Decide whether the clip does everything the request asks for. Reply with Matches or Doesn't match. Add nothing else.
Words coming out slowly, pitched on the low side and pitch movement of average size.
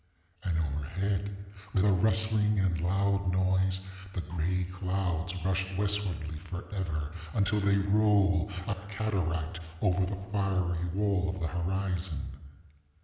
Doesn't match